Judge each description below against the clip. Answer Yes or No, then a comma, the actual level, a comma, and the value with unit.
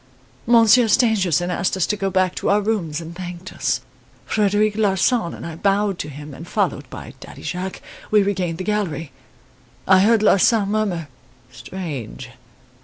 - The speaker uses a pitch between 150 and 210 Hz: Yes, high, 190 Hz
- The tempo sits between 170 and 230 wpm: No, average, 160 wpm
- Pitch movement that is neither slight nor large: Yes, average, 3.5 semitones